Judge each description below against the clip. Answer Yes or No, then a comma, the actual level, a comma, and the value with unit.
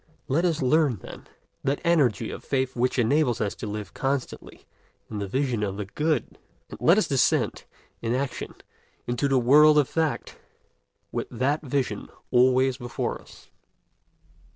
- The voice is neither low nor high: No, low, 130 Hz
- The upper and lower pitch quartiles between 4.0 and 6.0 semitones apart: No, average, 3.5 semitones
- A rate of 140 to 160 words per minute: Yes, average, 155 wpm